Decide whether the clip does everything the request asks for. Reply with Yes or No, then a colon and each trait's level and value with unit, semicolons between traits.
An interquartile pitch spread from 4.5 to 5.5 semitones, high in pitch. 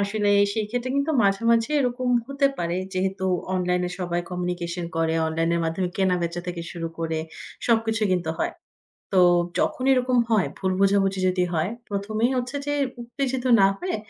Yes: average, 4.8 semitones; high, 195 Hz